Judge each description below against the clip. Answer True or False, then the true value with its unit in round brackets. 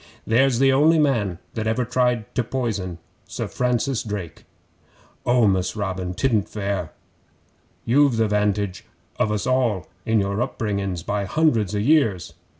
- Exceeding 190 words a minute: False (145 wpm)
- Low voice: True (110 Hz)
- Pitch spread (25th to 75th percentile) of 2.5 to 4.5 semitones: True (4.1 semitones)